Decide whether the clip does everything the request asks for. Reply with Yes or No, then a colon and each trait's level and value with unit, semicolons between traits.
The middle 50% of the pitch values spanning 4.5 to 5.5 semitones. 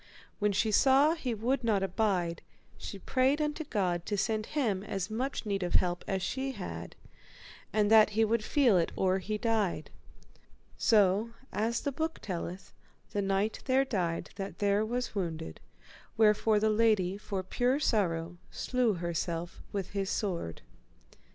No: average, 3.7 semitones